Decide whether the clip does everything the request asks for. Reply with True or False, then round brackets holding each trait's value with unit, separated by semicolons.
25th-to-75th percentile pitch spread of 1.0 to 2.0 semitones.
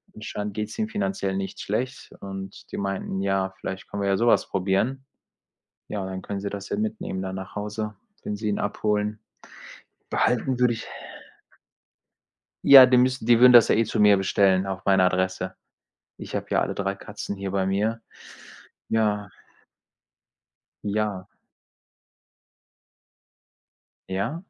False (2.7 semitones)